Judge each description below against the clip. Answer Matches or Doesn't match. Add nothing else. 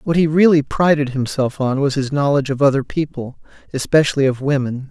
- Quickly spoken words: Doesn't match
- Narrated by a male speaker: Matches